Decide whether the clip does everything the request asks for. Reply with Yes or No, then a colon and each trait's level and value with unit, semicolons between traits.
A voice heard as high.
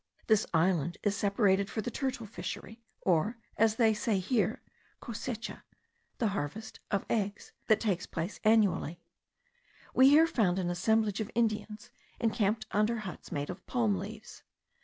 Yes: high, 215 Hz